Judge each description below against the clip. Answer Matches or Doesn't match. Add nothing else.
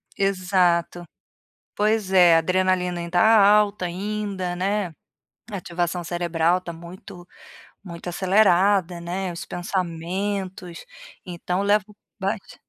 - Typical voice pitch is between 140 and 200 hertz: Matches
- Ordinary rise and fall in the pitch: Doesn't match